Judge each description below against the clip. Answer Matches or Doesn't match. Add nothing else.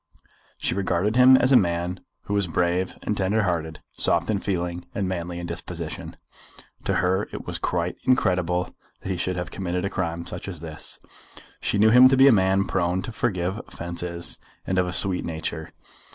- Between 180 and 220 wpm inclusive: Matches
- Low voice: Matches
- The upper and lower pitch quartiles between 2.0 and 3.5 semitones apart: Matches